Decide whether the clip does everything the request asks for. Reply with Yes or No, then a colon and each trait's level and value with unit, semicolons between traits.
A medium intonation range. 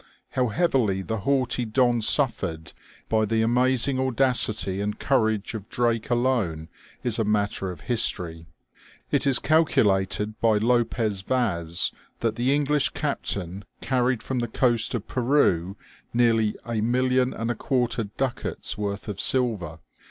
Yes: average, 3.7 semitones